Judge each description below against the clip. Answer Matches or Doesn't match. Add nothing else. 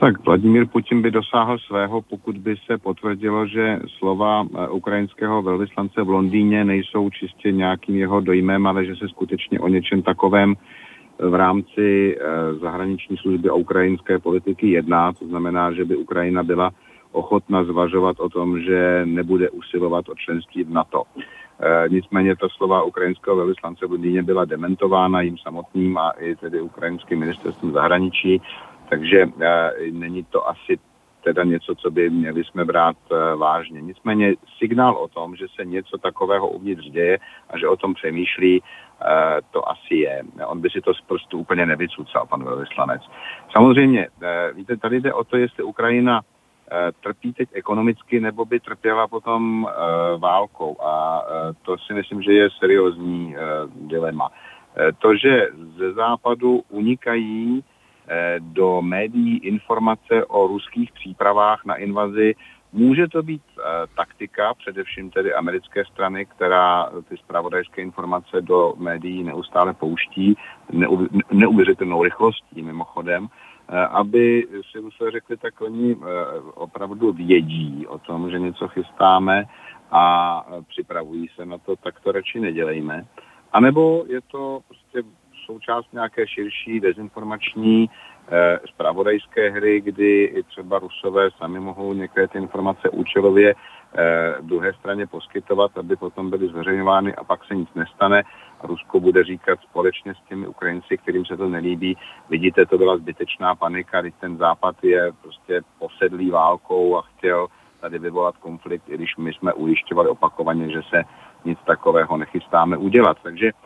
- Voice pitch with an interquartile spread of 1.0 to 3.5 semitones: Doesn't match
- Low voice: Matches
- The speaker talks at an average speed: Matches